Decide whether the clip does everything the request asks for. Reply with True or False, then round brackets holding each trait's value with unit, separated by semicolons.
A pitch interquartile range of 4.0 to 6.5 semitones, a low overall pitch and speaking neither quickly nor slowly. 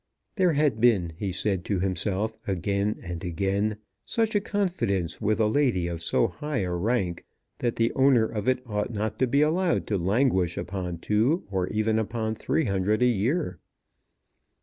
True (4.9 semitones; 110 Hz; 170 wpm)